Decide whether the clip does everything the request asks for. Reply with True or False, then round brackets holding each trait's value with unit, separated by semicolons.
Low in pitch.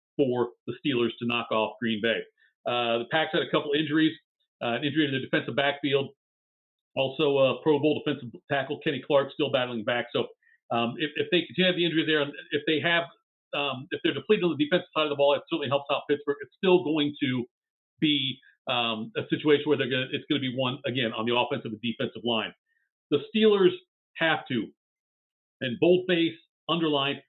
False (145 Hz)